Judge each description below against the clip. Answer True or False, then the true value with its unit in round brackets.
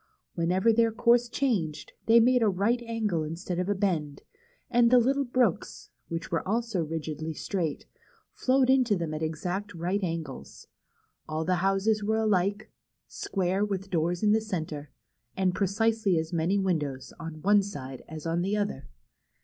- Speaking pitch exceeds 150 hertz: True (190 Hz)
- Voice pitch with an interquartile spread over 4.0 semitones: True (5.1 semitones)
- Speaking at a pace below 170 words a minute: True (160 wpm)